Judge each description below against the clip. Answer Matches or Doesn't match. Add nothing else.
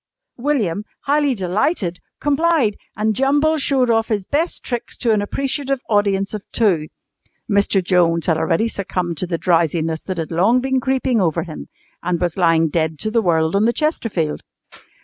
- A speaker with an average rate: Matches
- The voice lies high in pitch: Matches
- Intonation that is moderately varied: Doesn't match